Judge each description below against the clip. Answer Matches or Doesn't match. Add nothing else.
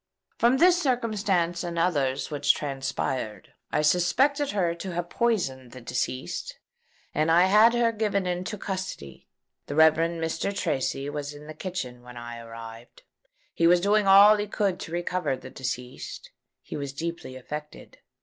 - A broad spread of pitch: Matches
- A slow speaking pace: Doesn't match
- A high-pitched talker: Doesn't match